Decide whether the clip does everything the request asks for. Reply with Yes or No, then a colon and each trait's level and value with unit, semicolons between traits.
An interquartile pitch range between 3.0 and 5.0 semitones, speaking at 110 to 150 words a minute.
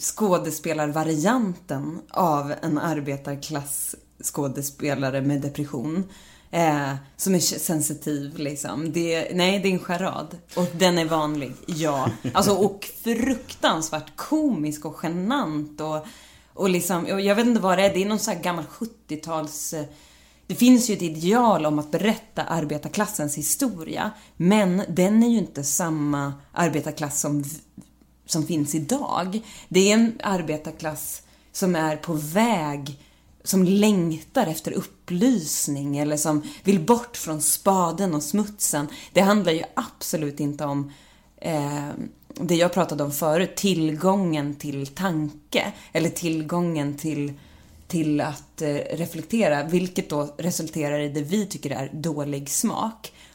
Yes: average, 4.3 semitones; average, 135 wpm